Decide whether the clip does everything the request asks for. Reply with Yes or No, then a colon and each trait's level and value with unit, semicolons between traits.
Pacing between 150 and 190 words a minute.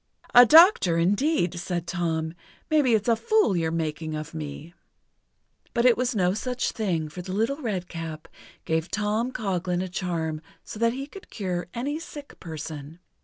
Yes: average, 165 wpm